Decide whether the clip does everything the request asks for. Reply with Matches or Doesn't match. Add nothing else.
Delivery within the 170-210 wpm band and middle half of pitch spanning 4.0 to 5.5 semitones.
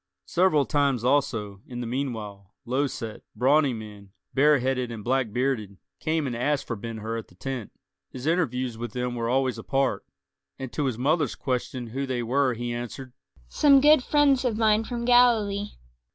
Matches